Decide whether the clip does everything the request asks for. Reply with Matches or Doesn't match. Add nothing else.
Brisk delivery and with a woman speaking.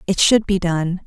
Matches